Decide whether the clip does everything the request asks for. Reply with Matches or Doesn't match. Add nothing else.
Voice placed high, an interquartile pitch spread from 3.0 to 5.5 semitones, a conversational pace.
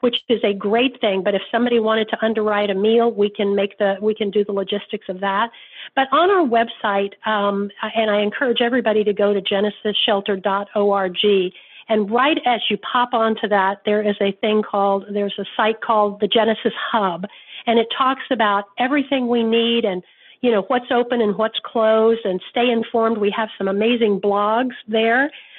Doesn't match